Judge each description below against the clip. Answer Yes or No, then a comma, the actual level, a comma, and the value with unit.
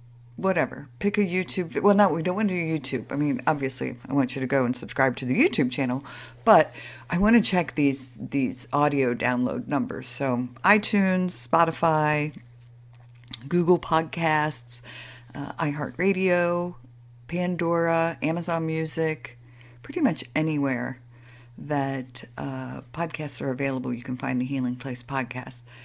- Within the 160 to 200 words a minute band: No, average, 140 wpm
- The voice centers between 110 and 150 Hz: Yes, medium, 140 Hz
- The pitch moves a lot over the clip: No, average, 5.0 semitones